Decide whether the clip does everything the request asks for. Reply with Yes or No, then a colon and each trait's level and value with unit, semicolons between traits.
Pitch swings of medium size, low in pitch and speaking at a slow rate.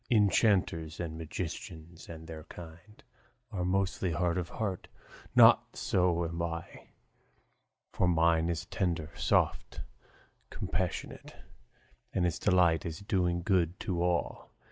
No: narrow, 1.9 semitones; very low, 85 Hz; slow, 120 wpm